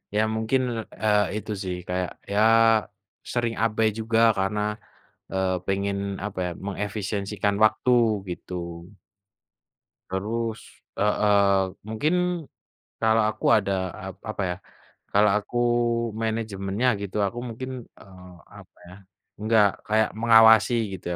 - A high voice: No, low, 105 Hz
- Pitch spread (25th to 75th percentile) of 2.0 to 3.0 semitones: Yes, narrow, 2.4 semitones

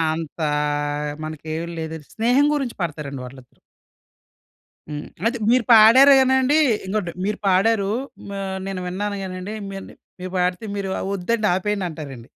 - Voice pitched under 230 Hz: Yes, high, 190 Hz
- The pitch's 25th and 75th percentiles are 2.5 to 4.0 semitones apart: No, wide, 5.5 semitones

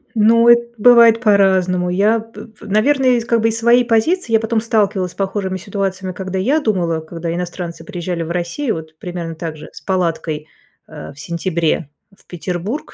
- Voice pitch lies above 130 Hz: Yes, high, 190 Hz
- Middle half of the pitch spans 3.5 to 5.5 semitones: Yes, average, 4.7 semitones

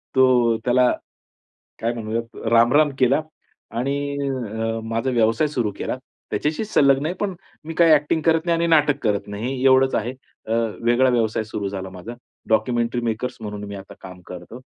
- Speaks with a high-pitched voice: No, low, 120 Hz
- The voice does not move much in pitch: No, average, 4.2 semitones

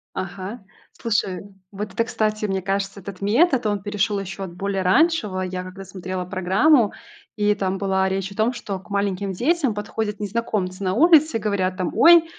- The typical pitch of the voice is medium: No, high, 200 Hz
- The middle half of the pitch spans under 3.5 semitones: Yes, narrow, 2.4 semitones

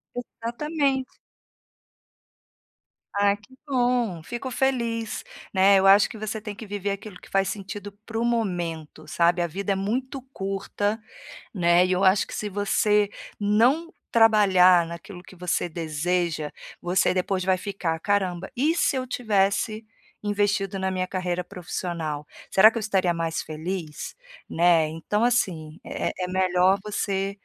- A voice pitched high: Yes, high, 195 Hz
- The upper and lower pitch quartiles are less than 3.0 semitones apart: No, average, 3.3 semitones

